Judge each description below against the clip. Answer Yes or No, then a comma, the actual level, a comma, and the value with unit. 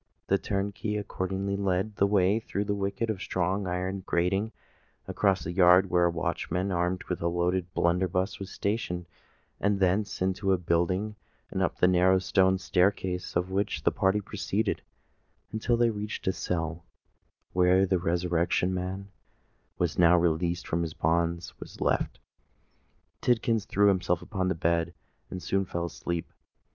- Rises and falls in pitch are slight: Yes, narrow, 2.0 semitones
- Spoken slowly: No, average, 155 wpm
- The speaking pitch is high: No, very low, 95 Hz